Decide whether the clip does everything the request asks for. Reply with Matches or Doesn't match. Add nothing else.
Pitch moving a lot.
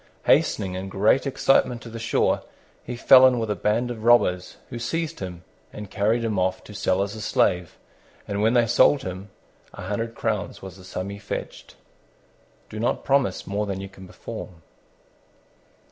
Doesn't match